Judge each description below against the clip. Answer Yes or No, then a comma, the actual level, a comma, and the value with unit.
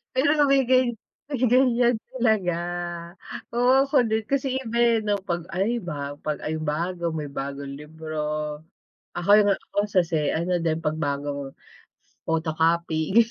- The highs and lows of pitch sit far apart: Yes, wide, 7.5 semitones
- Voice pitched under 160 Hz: No, medium, 175 Hz